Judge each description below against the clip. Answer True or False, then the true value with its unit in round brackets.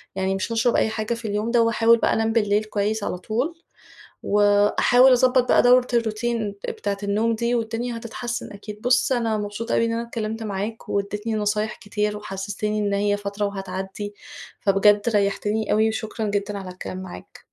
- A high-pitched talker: True (215 Hz)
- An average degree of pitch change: False (2.1 semitones)